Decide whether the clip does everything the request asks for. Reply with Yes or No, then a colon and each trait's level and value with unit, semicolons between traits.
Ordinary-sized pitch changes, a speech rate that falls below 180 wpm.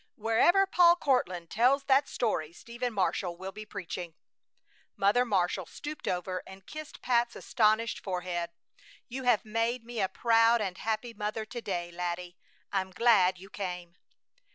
Yes: average, 4.7 semitones; average, 150 wpm